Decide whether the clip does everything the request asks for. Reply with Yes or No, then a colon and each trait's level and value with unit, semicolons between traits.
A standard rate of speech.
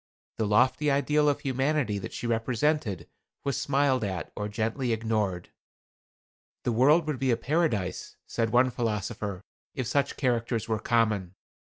Yes: average, 145 wpm